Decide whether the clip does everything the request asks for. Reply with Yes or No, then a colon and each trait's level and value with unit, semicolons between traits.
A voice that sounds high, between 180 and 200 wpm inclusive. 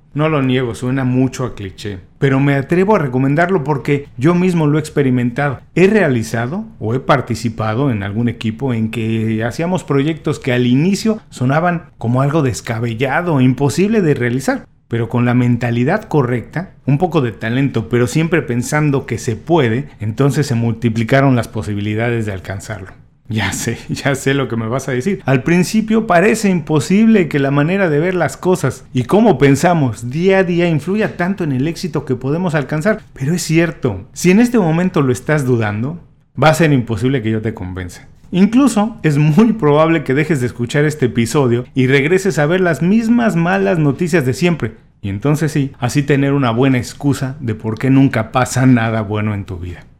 No: medium, 140 Hz; average, 185 wpm